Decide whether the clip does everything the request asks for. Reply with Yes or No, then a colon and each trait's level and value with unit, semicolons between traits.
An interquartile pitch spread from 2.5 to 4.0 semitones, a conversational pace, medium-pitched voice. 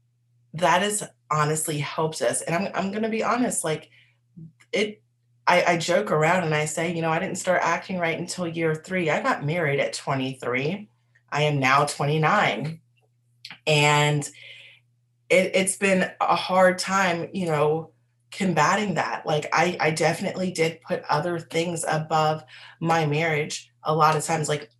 Yes: average, 3.5 semitones; average, 160 wpm; medium, 155 Hz